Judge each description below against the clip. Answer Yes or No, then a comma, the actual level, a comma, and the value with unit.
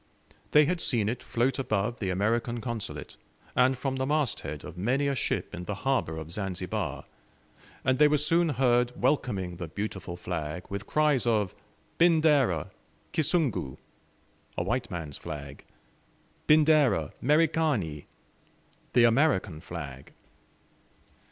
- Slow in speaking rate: Yes, slow, 130 wpm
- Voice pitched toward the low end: Yes, low, 120 Hz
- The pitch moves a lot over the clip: Yes, wide, 8.0 semitones